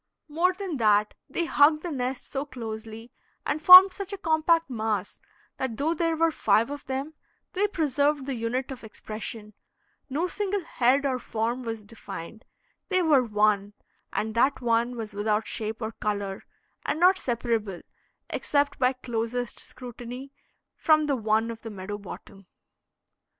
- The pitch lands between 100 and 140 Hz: No, very high, 250 Hz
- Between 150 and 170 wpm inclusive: Yes, average, 155 wpm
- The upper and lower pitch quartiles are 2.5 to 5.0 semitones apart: No, wide, 5.6 semitones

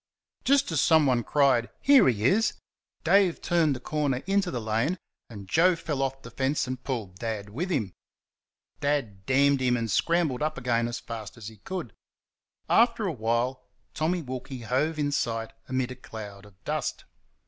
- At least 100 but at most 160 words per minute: No, average, 170 wpm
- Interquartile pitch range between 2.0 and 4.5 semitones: No, average, 5.3 semitones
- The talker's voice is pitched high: No, low, 130 Hz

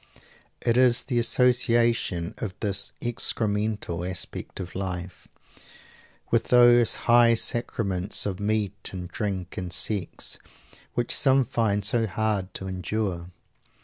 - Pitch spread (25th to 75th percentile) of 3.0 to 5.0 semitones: Yes, average, 4.0 semitones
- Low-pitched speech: Yes, low, 105 Hz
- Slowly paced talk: Yes, slow, 115 wpm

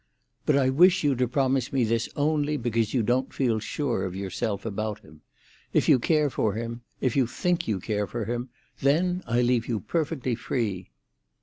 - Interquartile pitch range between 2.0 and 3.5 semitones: No, average, 4.0 semitones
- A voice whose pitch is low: Yes, low, 120 Hz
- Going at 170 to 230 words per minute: Yes, average, 180 wpm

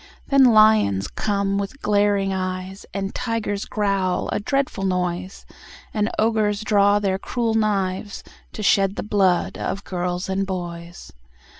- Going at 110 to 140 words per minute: Yes, slow, 135 wpm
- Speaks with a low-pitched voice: No, high, 200 Hz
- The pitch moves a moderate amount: No, narrow, 2.3 semitones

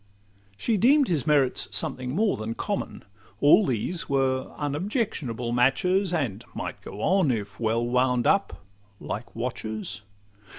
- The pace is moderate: No, slow, 130 wpm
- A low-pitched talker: Yes, low, 130 Hz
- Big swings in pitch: Yes, wide, 7.5 semitones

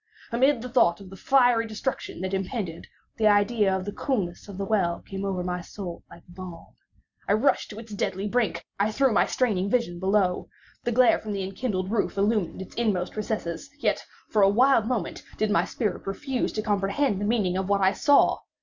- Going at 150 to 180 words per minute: No, average, 200 wpm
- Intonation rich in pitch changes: No, average, 3.4 semitones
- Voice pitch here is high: Yes, high, 205 Hz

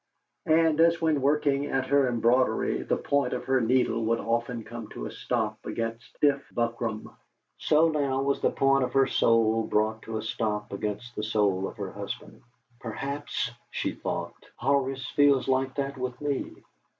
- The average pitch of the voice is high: No, low, 130 Hz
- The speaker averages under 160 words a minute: No, average, 175 wpm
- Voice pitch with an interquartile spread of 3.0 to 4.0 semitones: Yes, average, 3.4 semitones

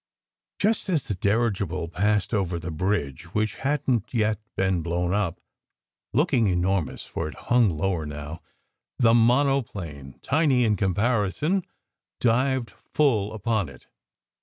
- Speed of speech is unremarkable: No, slow, 130 wpm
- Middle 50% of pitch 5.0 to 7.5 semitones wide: Yes, wide, 5.6 semitones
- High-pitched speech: No, low, 105 Hz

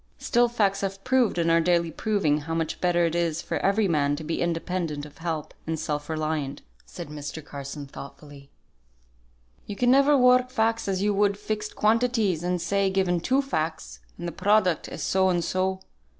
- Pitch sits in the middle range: Yes, medium, 175 Hz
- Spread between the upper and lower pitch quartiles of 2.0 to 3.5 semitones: No, average, 4.7 semitones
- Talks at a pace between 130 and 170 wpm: No, average, 185 wpm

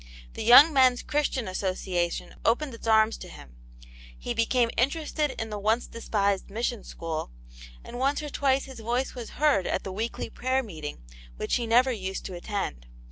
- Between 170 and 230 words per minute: Yes, average, 175 wpm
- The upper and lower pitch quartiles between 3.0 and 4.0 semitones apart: No, average, 4.8 semitones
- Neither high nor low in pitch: No, high, 230 Hz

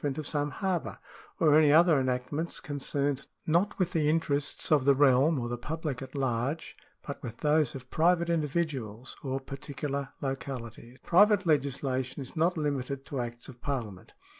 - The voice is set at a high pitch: No, medium, 140 Hz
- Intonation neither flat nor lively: Yes, average, 3.3 semitones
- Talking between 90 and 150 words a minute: No, average, 175 wpm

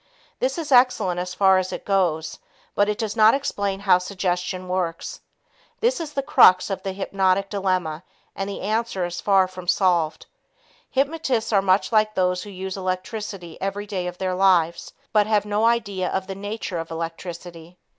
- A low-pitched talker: No, high, 190 Hz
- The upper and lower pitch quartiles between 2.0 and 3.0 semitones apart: Yes, narrow, 2.5 semitones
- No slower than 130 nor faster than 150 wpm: No, average, 175 wpm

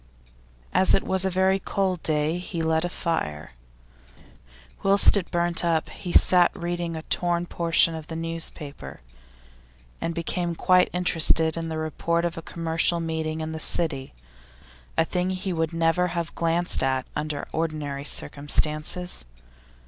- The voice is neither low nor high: Yes, medium, 165 Hz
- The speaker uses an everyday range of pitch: No, narrow, 1.8 semitones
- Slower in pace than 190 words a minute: Yes, average, 150 wpm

